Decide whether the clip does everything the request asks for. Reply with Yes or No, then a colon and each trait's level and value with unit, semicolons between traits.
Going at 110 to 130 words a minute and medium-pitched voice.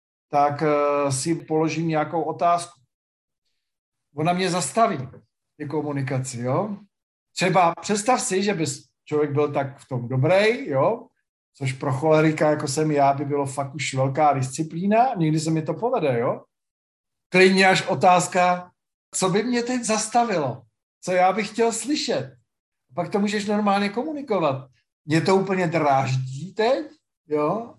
No: average, 140 wpm; medium, 155 Hz